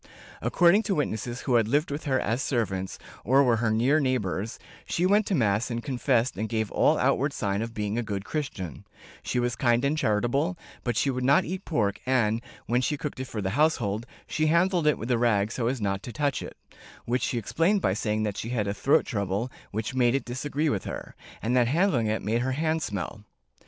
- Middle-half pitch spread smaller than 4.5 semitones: No, average, 4.8 semitones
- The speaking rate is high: Yes, fast, 220 wpm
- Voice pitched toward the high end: No, low, 120 Hz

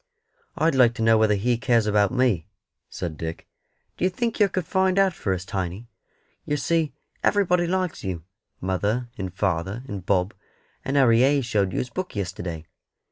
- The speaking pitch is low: Yes, low, 115 Hz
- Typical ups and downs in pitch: No, wide, 8.6 semitones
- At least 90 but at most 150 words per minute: No, average, 175 wpm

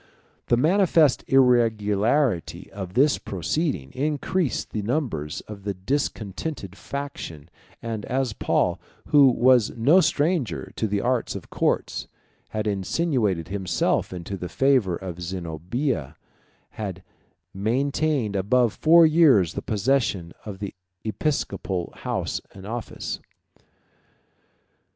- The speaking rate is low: Yes, slow, 110 wpm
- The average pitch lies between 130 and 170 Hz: No, low, 110 Hz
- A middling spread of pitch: No, wide, 6.5 semitones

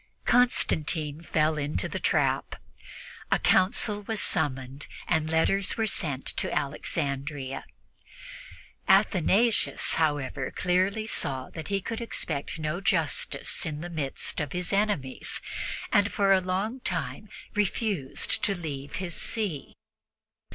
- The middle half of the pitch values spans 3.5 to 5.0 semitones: No, wide, 5.4 semitones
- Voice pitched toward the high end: No, medium, 165 Hz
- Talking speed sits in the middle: No, slow, 120 wpm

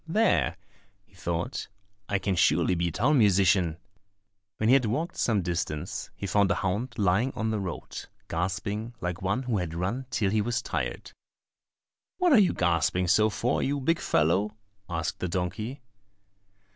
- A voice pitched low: Yes, low, 100 Hz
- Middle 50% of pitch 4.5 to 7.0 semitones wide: Yes, average, 5.1 semitones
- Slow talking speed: No, average, 160 wpm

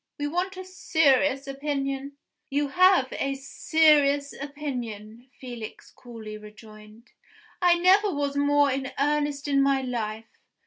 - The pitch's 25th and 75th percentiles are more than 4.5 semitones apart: No, average, 2.9 semitones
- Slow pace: Yes, slow, 125 wpm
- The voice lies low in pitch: No, very high, 275 Hz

